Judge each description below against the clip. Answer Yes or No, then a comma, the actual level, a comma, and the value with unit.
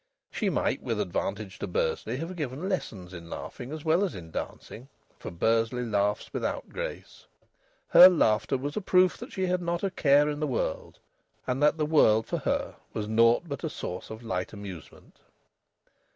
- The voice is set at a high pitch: No, low, 135 Hz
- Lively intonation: Yes, wide, 7.5 semitones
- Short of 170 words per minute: No, average, 180 wpm